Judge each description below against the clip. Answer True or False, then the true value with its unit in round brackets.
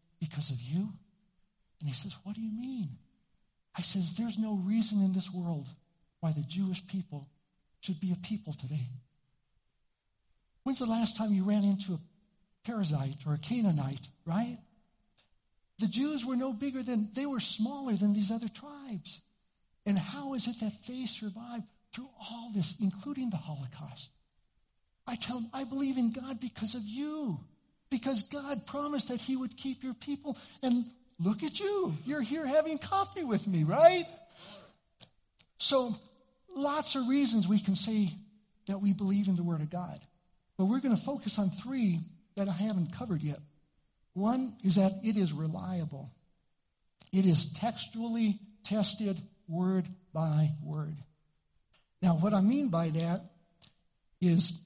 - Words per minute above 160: False (155 wpm)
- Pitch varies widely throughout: True (5.9 semitones)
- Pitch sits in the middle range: False (205 Hz)